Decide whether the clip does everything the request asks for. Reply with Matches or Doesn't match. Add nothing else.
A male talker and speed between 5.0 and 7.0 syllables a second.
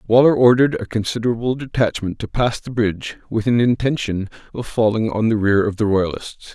Matches